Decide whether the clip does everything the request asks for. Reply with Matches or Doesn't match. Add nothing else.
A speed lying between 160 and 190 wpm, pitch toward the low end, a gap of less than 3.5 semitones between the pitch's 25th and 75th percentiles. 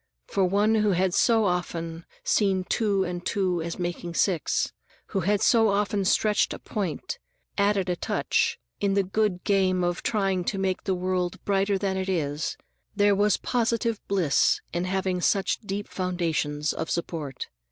Doesn't match